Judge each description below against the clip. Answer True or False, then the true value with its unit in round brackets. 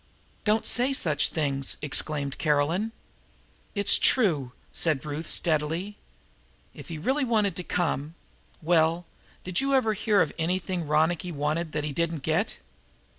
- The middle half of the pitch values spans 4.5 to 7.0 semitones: True (4.9 semitones)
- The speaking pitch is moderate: True (165 Hz)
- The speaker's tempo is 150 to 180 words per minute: False (140 wpm)